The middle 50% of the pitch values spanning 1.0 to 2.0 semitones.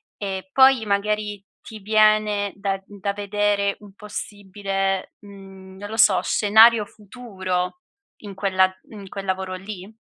Yes: narrow, 1.6 semitones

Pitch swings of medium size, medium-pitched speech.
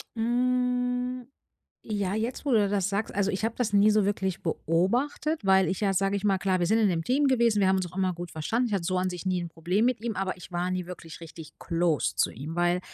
No: average, 4.1 semitones; high, 195 Hz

